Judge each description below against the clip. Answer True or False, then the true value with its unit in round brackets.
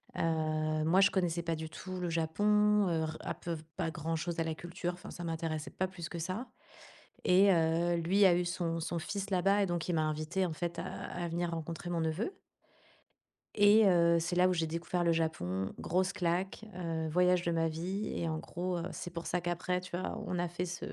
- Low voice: False (170 Hz)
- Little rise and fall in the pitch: True (1.9 semitones)